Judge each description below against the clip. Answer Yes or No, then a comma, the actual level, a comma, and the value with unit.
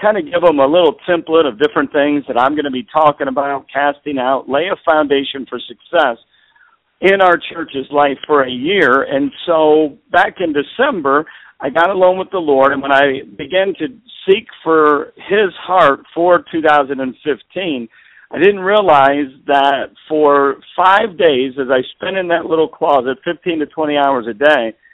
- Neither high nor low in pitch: Yes, medium, 150 Hz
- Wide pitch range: No, average, 4.1 semitones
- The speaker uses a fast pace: No, average, 175 wpm